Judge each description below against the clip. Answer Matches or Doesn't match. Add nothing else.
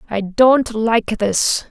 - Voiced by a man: Doesn't match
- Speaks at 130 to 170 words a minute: Matches